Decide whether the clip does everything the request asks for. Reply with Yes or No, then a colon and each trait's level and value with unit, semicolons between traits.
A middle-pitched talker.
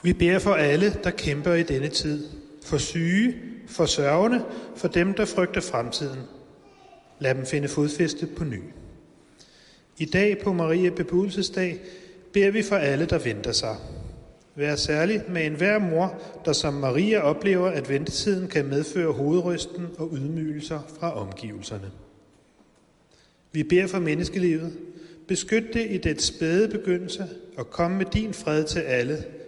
Yes: medium, 170 Hz